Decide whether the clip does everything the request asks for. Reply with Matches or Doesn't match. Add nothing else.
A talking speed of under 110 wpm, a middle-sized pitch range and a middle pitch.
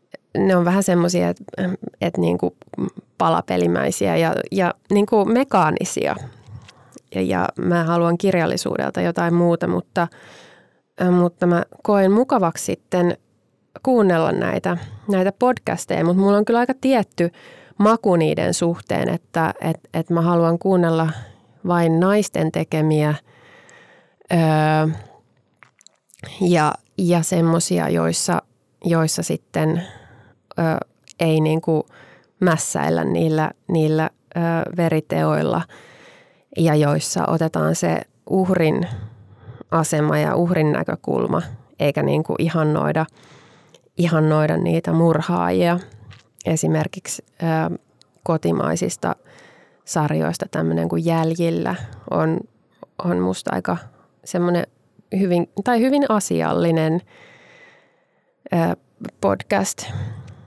Doesn't match